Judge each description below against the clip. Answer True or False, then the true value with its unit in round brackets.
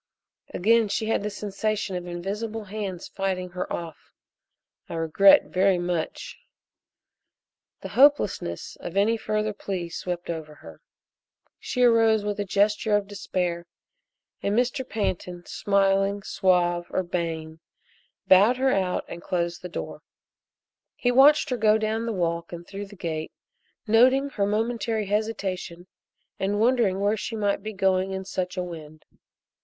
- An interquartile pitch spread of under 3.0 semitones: False (3.5 semitones)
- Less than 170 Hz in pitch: False (195 Hz)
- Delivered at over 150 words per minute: False (145 wpm)